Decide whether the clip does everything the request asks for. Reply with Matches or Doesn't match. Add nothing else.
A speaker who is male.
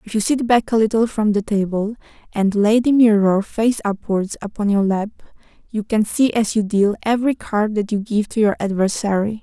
Doesn't match